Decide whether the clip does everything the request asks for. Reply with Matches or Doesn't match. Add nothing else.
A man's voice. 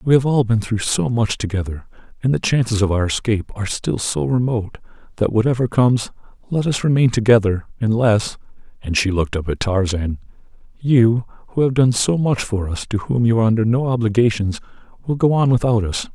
Matches